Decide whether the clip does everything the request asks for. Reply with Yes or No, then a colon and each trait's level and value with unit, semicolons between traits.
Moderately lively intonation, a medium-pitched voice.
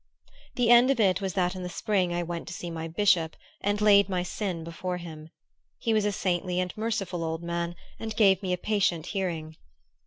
Yes: average, 3.1 semitones; medium, 180 Hz